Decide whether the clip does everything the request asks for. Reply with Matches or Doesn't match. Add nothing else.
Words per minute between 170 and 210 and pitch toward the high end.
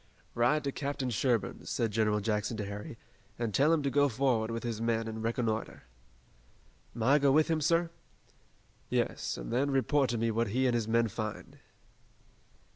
Doesn't match